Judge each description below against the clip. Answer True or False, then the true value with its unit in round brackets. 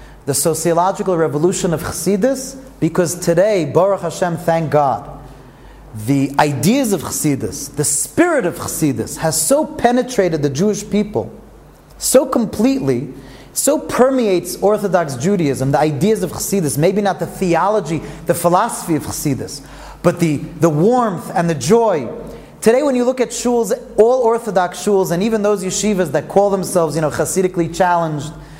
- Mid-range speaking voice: True (175 Hz)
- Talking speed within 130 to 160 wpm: True (145 wpm)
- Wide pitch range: True (5.7 semitones)